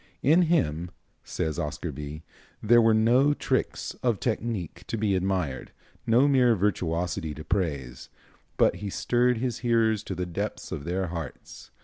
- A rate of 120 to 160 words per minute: Yes, average, 150 wpm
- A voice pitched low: Yes, very low, 95 Hz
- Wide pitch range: Yes, wide, 6.3 semitones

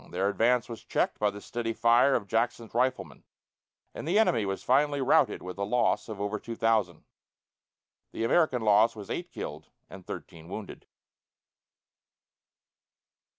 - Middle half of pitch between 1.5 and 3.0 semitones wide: No, average, 3.4 semitones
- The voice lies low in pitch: Yes, low, 115 Hz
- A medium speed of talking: Yes, average, 150 wpm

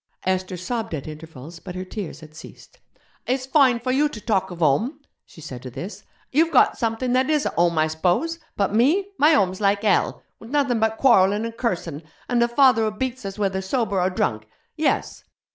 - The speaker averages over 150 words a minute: Yes, fast, 205 wpm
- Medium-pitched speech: No, high, 210 Hz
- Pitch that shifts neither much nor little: No, wide, 6.3 semitones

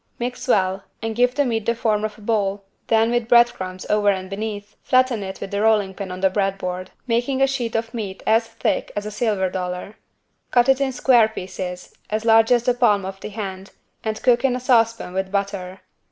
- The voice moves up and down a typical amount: Yes, average, 3.5 semitones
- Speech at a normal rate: No, fast, 220 wpm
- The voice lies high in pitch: Yes, high, 215 Hz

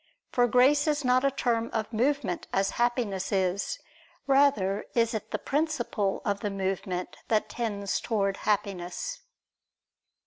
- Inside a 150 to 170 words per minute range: No, slow, 135 wpm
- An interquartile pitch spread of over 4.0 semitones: Yes, average, 4.5 semitones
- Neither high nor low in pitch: No, high, 225 Hz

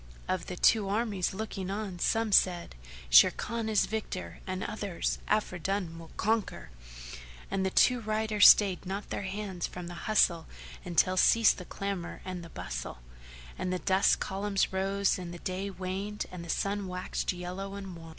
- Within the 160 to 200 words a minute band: Yes, average, 165 wpm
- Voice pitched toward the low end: No, high, 190 Hz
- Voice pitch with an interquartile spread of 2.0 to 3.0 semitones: Yes, narrow, 2.4 semitones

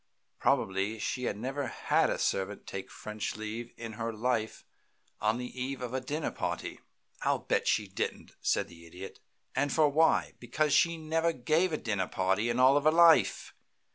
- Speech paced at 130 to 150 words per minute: No, average, 170 wpm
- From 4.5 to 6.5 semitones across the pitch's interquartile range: Yes, average, 5.3 semitones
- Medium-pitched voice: No, low, 120 Hz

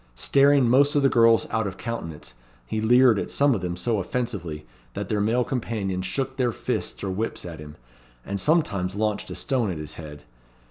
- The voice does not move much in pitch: No, average, 5.2 semitones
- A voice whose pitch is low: Yes, low, 110 Hz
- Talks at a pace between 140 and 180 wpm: No, average, 195 wpm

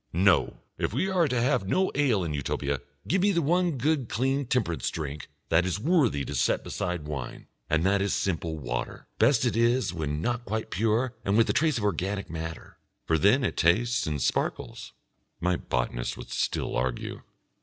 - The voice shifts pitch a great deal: Yes, wide, 8.1 semitones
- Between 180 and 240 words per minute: Yes, average, 185 wpm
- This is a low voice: Yes, low, 100 Hz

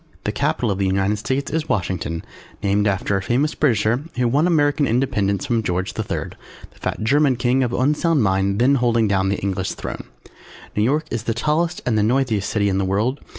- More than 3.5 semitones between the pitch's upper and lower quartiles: Yes, wide, 5.5 semitones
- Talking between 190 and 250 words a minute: Yes, fast, 205 wpm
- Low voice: Yes, low, 115 Hz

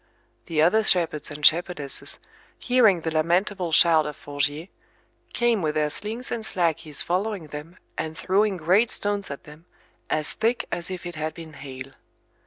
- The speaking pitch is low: No, medium, 170 Hz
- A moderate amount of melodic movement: Yes, average, 4.5 semitones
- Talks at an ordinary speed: Yes, average, 160 wpm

